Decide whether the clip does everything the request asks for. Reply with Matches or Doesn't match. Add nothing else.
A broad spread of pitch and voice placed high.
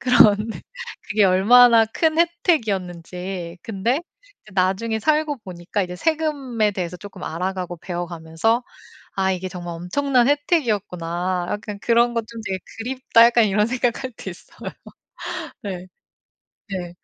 Doesn't match